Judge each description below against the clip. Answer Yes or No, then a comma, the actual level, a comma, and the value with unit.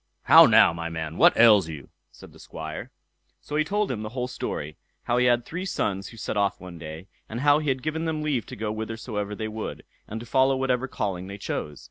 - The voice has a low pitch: Yes, low, 110 Hz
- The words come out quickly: Yes, fast, 230 wpm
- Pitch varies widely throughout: Yes, wide, 5.7 semitones